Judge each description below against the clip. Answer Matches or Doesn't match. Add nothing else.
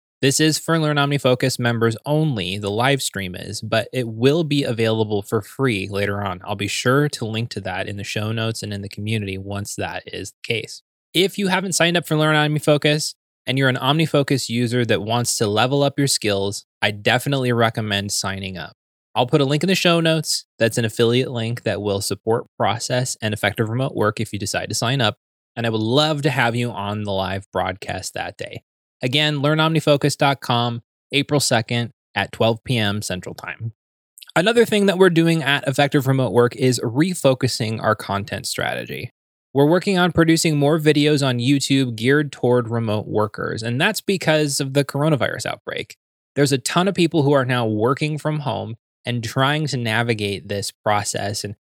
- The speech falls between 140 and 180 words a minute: Doesn't match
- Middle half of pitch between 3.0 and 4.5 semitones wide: Doesn't match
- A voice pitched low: Matches